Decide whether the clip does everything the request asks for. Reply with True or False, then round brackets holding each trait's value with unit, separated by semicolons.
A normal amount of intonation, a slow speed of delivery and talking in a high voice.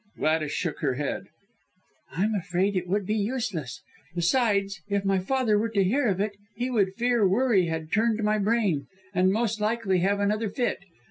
False (3.4 semitones; 180 wpm; 200 Hz)